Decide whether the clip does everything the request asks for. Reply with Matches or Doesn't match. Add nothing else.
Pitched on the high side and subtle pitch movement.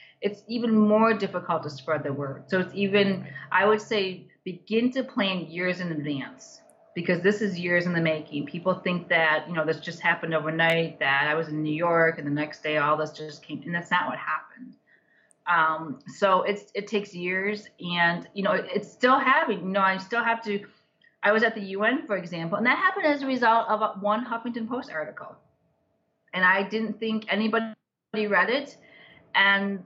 Doesn't match